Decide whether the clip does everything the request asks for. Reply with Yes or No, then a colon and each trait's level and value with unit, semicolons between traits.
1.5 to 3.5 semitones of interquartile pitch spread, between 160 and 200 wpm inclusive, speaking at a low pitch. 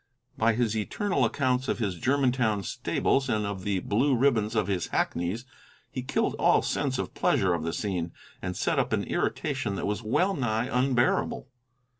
No: average, 4.3 semitones; average, 175 wpm; low, 110 Hz